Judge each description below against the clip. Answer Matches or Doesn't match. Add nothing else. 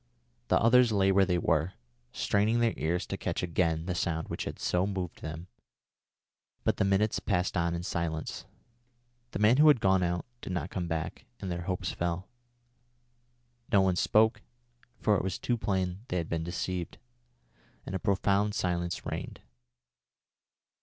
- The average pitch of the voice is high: Doesn't match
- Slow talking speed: Doesn't match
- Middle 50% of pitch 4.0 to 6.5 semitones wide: Doesn't match